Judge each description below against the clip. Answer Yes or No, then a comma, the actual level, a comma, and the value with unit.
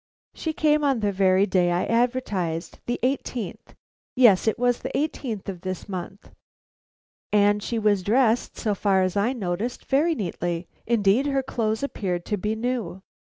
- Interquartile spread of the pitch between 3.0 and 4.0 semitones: No, average, 4.7 semitones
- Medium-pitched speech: No, high, 215 Hz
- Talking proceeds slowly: No, average, 160 wpm